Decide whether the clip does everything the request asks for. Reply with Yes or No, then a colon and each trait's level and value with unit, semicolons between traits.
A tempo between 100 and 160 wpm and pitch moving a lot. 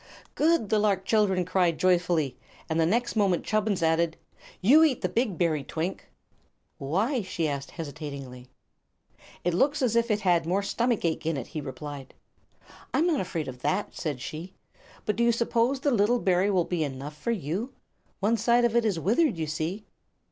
No: average, 185 wpm; wide, 6.3 semitones